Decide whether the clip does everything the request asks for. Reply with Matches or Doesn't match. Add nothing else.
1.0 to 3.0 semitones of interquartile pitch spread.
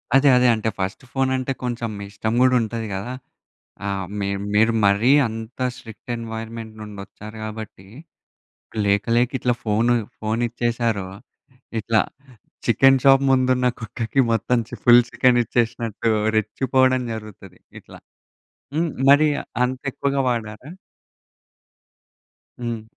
Matches